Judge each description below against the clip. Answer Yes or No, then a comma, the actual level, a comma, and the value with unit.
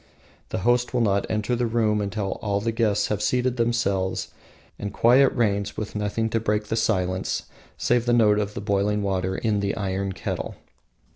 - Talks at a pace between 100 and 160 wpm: No, average, 185 wpm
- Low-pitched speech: Yes, low, 105 Hz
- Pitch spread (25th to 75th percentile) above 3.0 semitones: No, narrow, 2.6 semitones